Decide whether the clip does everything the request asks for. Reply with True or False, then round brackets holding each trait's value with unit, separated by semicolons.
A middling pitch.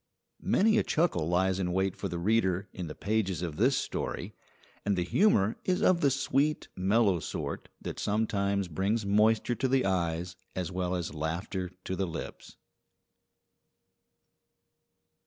False (95 Hz)